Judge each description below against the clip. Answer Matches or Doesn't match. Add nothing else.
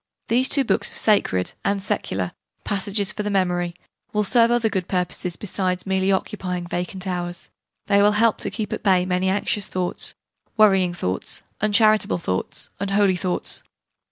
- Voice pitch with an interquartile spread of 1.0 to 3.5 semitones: Matches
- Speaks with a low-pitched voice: Doesn't match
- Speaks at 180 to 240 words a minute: Doesn't match